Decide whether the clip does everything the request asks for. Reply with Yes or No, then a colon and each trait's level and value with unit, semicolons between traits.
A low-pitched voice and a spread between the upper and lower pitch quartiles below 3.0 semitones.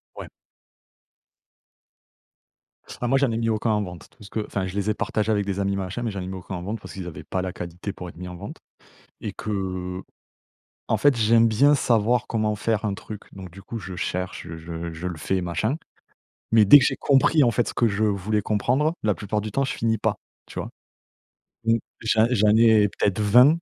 No: low, 105 Hz; average, 3.4 semitones